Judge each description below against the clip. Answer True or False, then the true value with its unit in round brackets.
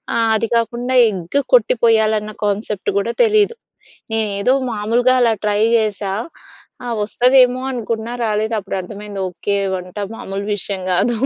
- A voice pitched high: True (215 Hz)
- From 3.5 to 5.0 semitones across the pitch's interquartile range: False (2.9 semitones)